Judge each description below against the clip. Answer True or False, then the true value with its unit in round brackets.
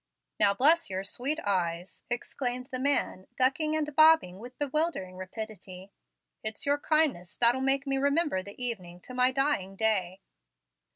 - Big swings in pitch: True (6.8 semitones)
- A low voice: False (250 Hz)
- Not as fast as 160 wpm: True (150 wpm)